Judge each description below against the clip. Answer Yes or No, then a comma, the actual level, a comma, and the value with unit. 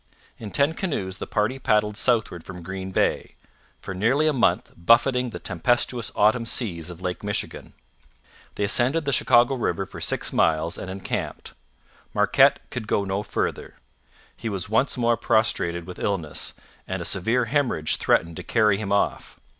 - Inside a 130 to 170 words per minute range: Yes, average, 160 wpm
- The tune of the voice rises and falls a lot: No, average, 4.5 semitones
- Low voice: Yes, low, 105 Hz